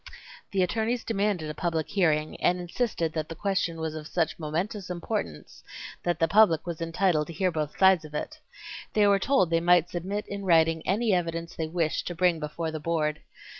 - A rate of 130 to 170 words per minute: No, average, 195 wpm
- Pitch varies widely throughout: No, average, 3.2 semitones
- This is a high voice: No, medium, 170 Hz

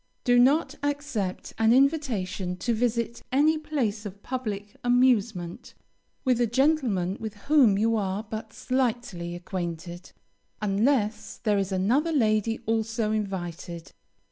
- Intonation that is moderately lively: Yes, average, 4.5 semitones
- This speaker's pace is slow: Yes, slow, 120 wpm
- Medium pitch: No, high, 220 Hz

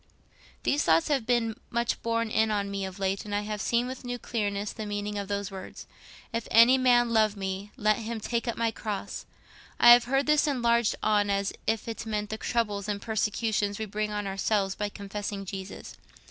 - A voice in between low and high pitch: No, high, 215 Hz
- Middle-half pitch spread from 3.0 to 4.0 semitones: No, narrow, 2.5 semitones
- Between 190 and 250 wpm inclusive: Yes, average, 200 wpm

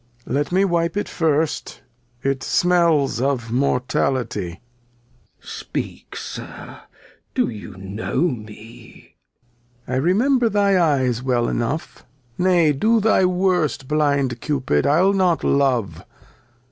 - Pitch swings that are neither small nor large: No, wide, 6.2 semitones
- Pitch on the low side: No, medium, 145 Hz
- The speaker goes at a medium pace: No, slow, 120 wpm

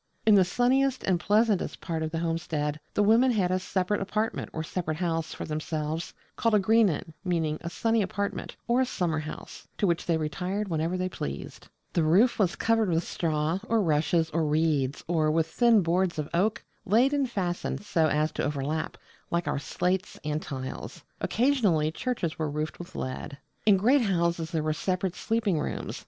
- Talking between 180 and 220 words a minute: Yes, average, 185 wpm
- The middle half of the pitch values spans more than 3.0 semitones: Yes, average, 4.7 semitones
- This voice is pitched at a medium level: Yes, medium, 175 Hz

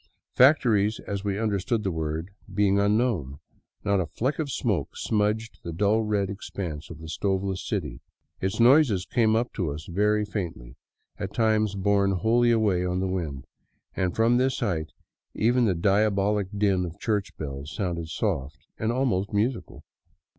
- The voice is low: Yes, low, 100 Hz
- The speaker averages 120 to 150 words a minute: No, average, 160 wpm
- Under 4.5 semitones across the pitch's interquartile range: Yes, average, 3.6 semitones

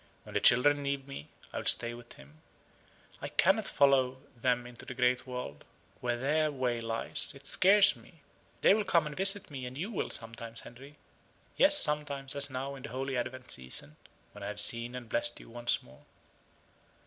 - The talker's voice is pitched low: Yes, low, 130 Hz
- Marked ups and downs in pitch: No, average, 3.1 semitones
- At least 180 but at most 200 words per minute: Yes, average, 190 wpm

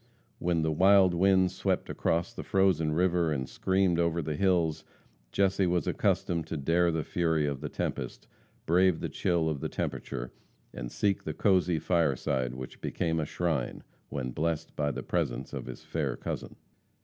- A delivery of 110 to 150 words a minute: No, average, 170 wpm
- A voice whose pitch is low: Yes, very low, 80 Hz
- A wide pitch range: No, average, 3.0 semitones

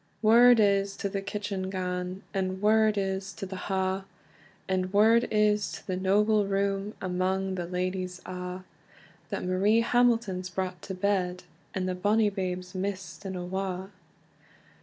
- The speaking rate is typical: Yes, average, 145 wpm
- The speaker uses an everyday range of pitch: No, narrow, 1.8 semitones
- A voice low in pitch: No, high, 190 Hz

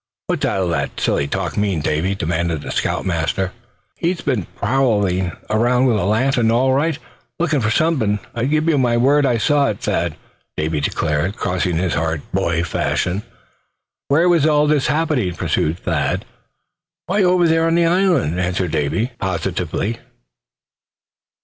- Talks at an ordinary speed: Yes, average, 155 wpm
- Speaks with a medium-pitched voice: No, low, 110 Hz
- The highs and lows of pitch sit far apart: Yes, wide, 8.7 semitones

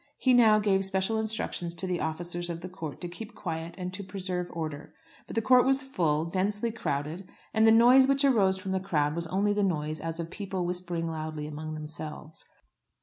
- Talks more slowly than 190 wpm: No, fast, 205 wpm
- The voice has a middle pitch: Yes, medium, 180 Hz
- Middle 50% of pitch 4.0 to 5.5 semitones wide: Yes, average, 4.3 semitones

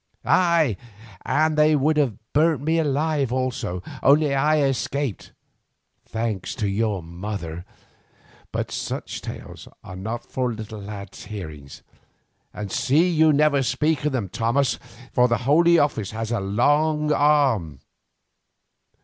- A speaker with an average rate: No, slow, 130 wpm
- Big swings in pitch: Yes, wide, 6.3 semitones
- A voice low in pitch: Yes, low, 130 Hz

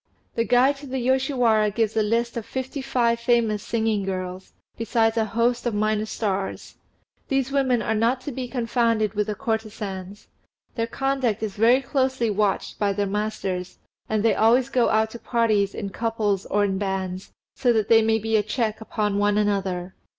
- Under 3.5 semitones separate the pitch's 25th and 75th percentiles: Yes, narrow, 2.6 semitones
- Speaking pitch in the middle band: No, high, 220 Hz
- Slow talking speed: No, average, 180 wpm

